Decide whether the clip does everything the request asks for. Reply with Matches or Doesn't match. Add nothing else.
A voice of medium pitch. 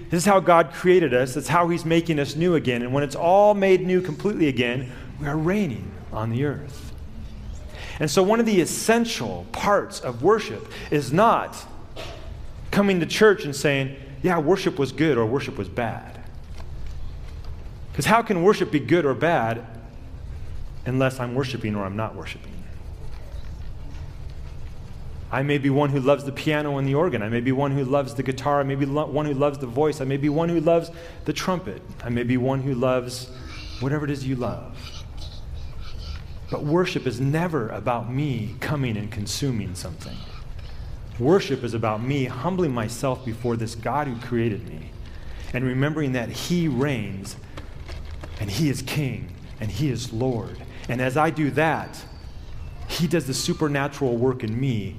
Doesn't match